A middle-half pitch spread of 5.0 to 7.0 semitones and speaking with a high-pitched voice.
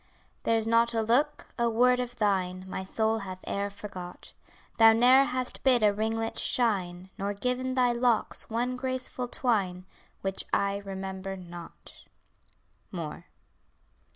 No: average, 4.2 semitones; high, 225 Hz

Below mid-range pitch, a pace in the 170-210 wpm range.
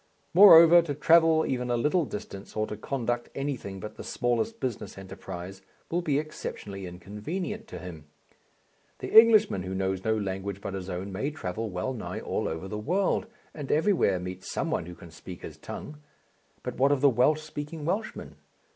Yes: low, 120 Hz; average, 180 wpm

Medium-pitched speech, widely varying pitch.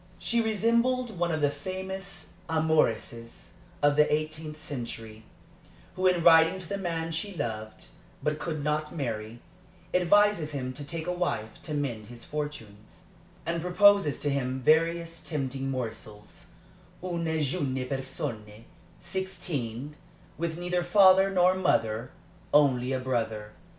Yes: medium, 150 Hz; wide, 5.7 semitones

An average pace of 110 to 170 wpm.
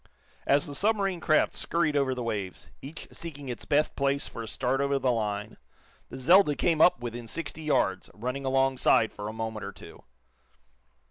No: average, 180 wpm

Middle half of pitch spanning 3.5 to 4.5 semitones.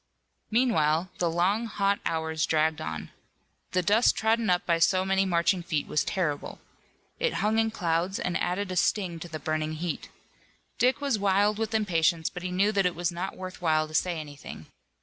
Yes: average, 3.9 semitones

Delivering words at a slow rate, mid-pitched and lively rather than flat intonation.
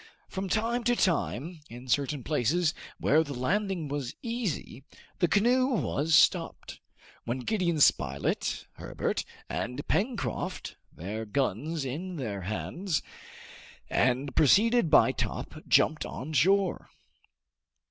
Yes: slow, 115 wpm; medium, 155 Hz; wide, 7.2 semitones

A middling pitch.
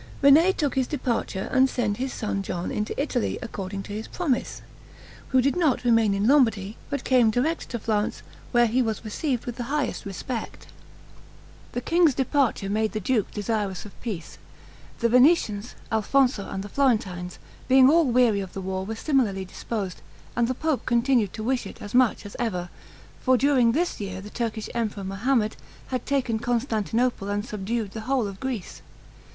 No: high, 230 Hz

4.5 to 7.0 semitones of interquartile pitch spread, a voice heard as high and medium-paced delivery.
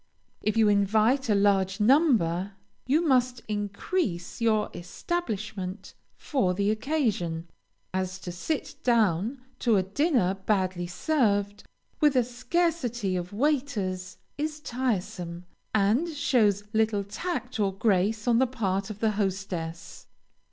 No: average, 5.1 semitones; high, 210 Hz; slow, 125 wpm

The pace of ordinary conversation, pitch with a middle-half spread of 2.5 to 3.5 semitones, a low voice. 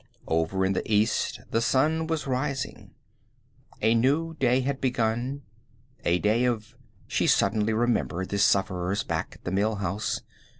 No: average, 145 wpm; average, 4.6 semitones; low, 110 Hz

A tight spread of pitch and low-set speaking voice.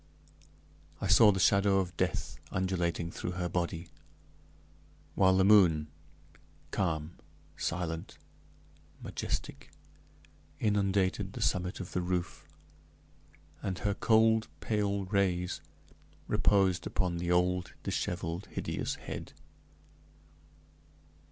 Yes: narrow, 2.2 semitones; very low, 90 Hz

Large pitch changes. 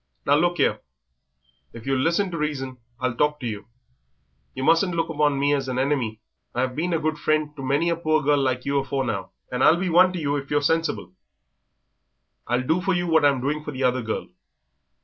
No: average, 3.8 semitones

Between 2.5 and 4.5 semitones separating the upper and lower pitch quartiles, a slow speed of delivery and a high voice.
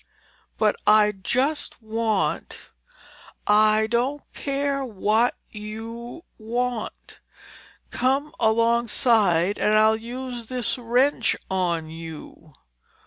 Yes: average, 2.8 semitones; slow, 85 wpm; high, 225 Hz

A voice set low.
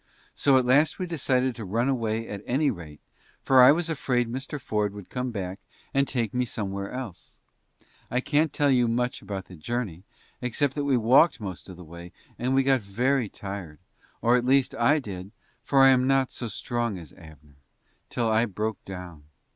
Yes: low, 120 Hz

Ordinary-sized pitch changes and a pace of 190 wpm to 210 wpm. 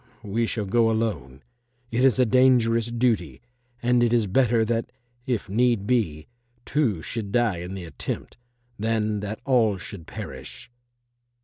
No: average, 3.3 semitones; average, 145 wpm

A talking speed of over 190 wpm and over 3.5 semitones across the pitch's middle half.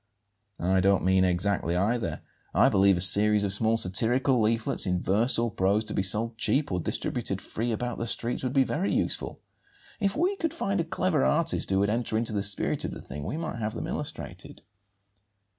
Yes: average, 200 wpm; average, 4.5 semitones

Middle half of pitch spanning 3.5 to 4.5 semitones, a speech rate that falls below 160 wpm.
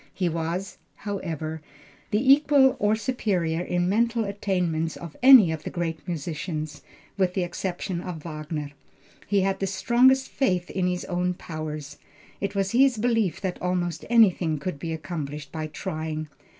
Yes: average, 4.1 semitones; average, 150 wpm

